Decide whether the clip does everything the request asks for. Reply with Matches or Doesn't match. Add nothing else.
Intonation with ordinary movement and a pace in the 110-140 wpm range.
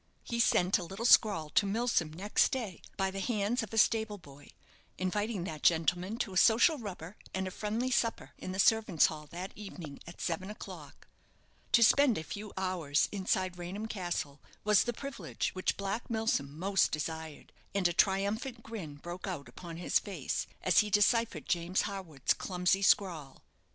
Doesn't match